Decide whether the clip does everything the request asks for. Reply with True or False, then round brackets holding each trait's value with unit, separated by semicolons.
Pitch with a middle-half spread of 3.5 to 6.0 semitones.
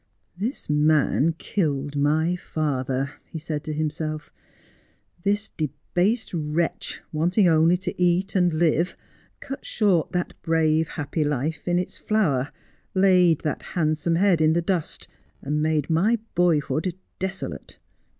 False (2.9 semitones)